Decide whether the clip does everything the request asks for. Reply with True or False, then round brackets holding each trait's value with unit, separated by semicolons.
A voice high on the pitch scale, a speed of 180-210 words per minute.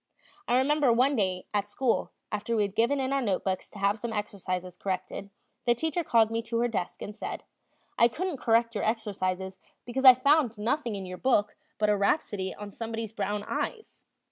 True (225 Hz; 195 wpm)